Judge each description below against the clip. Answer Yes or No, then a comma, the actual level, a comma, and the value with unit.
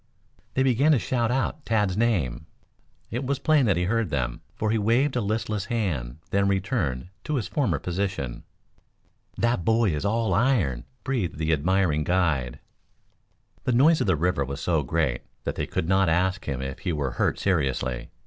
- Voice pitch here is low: Yes, very low, 95 Hz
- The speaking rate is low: No, average, 175 wpm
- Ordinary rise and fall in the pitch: No, wide, 7.4 semitones